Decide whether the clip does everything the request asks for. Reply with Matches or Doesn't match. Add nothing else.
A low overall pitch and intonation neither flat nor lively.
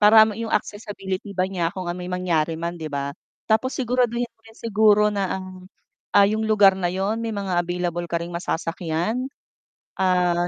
Doesn't match